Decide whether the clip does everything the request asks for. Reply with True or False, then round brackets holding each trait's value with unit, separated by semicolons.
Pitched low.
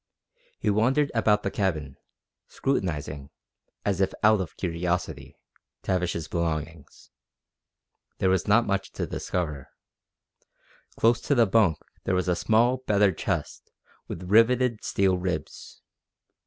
True (95 Hz)